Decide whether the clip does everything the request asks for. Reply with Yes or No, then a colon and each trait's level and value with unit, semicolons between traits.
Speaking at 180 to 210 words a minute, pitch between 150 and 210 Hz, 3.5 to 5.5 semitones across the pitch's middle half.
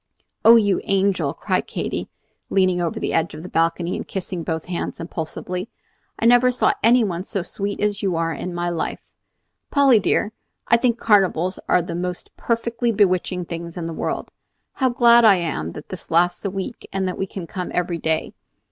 Yes: average, 190 wpm; medium, 185 Hz; average, 3.9 semitones